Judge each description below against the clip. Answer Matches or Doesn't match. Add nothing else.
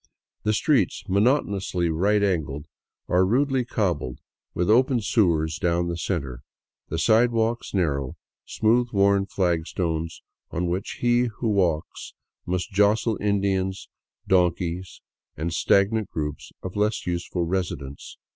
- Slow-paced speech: Matches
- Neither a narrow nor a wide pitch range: Matches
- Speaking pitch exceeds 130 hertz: Doesn't match